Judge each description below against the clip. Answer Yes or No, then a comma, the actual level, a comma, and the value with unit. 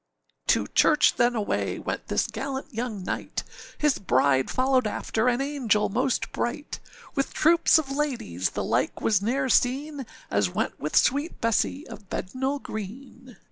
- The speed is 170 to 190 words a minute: No, average, 150 wpm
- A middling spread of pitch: Yes, average, 4.7 semitones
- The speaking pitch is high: Yes, very high, 250 Hz